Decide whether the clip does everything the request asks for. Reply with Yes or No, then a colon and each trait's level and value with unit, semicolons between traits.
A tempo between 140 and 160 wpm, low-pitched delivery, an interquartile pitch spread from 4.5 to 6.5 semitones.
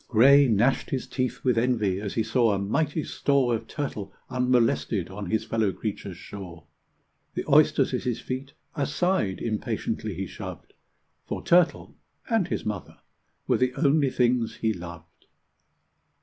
Yes: average, 150 wpm; low, 115 Hz; average, 4.9 semitones